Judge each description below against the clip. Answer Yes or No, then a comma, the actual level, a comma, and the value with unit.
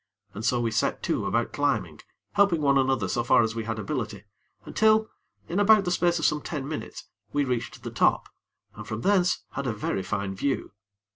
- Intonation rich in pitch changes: Yes, wide, 7.6 semitones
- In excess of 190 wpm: Yes, average, 200 wpm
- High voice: No, low, 135 Hz